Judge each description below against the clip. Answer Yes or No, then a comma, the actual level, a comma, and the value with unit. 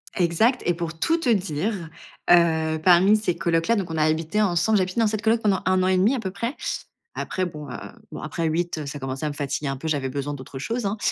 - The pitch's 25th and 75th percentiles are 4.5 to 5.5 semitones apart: Yes, average, 4.9 semitones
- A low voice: No, medium, 175 Hz